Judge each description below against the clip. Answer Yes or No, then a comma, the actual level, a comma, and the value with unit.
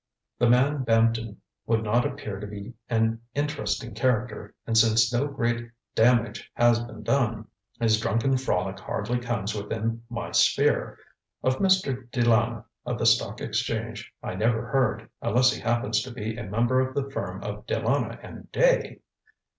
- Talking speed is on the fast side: No, average, 160 wpm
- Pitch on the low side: Yes, low, 115 Hz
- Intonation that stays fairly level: Yes, narrow, 2.2 semitones